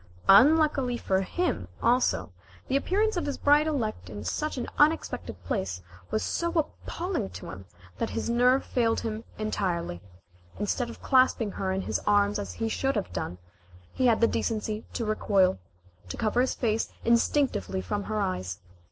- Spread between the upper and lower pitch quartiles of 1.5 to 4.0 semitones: No, average, 5.1 semitones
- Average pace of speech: Yes, average, 165 wpm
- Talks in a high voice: Yes, high, 225 Hz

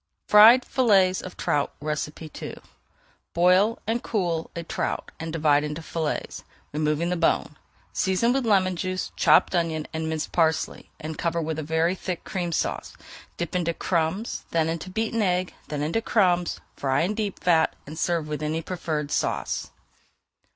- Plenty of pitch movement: No, average, 2.8 semitones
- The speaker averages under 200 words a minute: Yes, average, 160 wpm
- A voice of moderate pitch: Yes, medium, 170 Hz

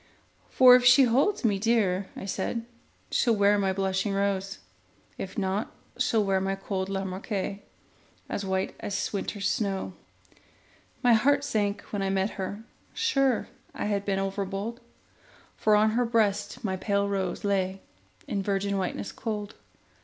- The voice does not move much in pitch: Yes, narrow, 2.3 semitones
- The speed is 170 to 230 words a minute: No, average, 145 wpm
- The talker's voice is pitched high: Yes, high, 200 Hz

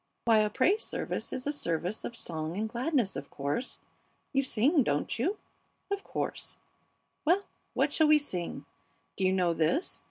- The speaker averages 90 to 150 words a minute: No, average, 165 wpm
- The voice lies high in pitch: Yes, high, 230 Hz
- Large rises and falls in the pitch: Yes, wide, 8.8 semitones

